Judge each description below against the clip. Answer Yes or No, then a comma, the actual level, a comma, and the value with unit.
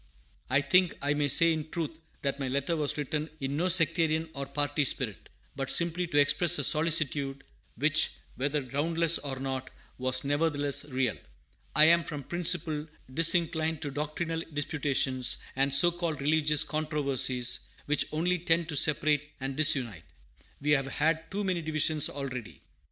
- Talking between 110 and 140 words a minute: No, average, 155 wpm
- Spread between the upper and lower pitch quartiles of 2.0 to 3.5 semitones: Yes, average, 2.9 semitones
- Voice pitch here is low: No, medium, 150 Hz